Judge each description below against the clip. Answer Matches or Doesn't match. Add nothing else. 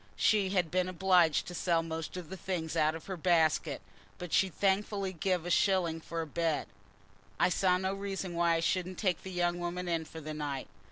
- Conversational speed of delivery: Doesn't match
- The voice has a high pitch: Doesn't match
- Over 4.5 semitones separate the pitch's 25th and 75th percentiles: Doesn't match